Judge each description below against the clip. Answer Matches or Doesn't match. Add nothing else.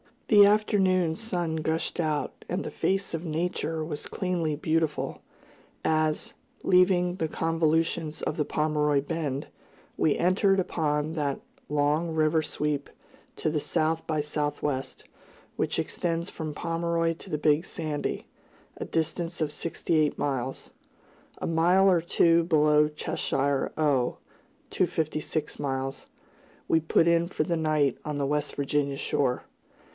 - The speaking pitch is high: Doesn't match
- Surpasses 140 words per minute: Doesn't match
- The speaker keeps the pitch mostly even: Matches